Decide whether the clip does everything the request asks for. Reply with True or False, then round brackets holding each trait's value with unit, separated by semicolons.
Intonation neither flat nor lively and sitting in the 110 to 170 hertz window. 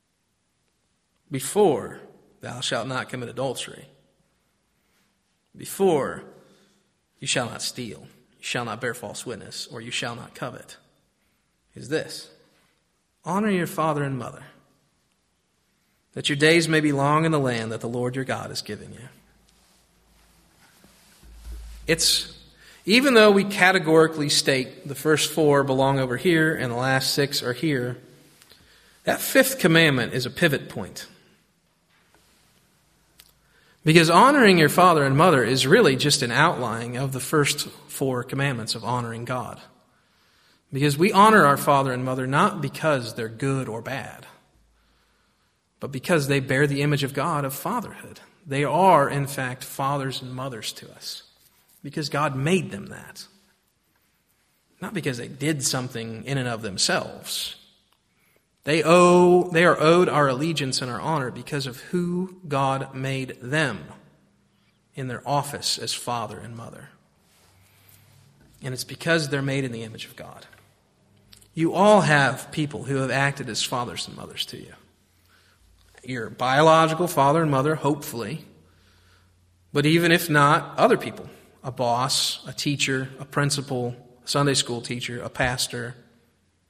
True (4.3 semitones; 135 Hz)